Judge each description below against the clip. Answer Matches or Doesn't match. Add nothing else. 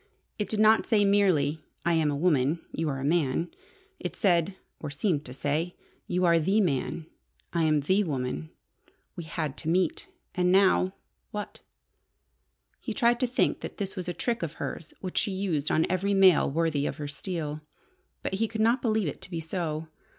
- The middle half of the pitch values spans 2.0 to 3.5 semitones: Doesn't match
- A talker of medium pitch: Matches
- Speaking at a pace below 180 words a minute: Doesn't match